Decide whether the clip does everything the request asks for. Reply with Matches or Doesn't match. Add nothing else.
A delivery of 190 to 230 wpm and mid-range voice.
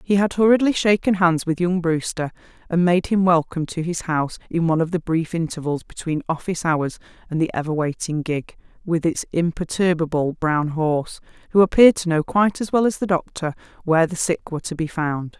Matches